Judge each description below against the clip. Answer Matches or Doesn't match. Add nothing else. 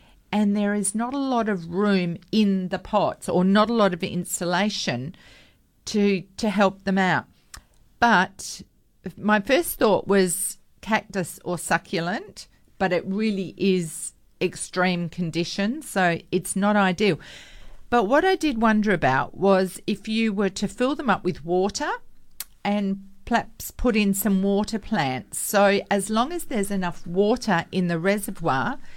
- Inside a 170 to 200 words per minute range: Doesn't match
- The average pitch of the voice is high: Matches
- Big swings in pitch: Doesn't match